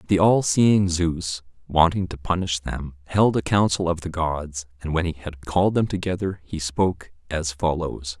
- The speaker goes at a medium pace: Yes, average, 185 wpm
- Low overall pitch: Yes, very low, 85 Hz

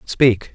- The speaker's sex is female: No, male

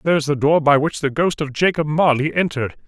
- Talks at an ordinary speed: No, fast, 230 wpm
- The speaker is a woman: No, male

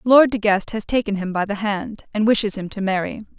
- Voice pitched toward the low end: No, high, 210 Hz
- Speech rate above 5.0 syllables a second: Yes, 5.4 syllables/s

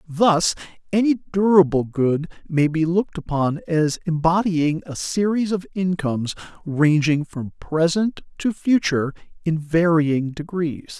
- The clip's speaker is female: No, male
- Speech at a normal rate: No, slow, 120 wpm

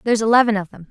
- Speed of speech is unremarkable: No, fast, 265 wpm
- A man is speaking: No, female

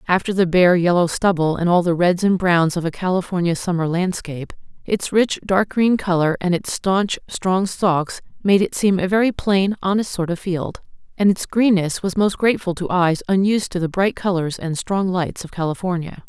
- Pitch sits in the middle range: Yes, medium, 180 Hz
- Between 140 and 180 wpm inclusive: No, average, 200 wpm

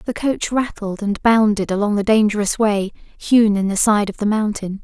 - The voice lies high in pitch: Yes, high, 210 Hz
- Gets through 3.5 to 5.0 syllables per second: Yes, 4.7 syllables/s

